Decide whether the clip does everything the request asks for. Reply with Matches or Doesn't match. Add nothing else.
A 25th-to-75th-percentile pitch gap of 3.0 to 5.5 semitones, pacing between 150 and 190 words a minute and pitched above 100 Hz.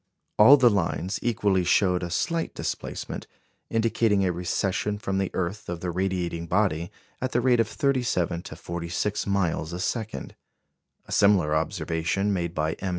Doesn't match